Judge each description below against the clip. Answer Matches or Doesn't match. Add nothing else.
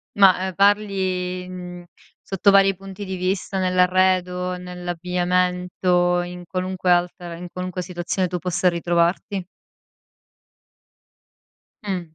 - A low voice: Doesn't match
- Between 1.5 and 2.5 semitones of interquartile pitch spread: Doesn't match